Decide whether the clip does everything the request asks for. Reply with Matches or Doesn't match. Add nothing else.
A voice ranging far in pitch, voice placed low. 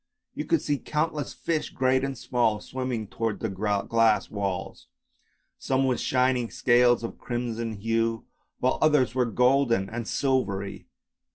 Doesn't match